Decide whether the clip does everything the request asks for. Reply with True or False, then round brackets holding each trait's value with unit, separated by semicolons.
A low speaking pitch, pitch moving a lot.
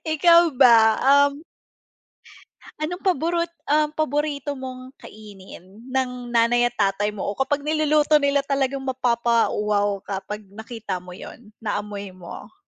False (255 Hz; 5.8 semitones)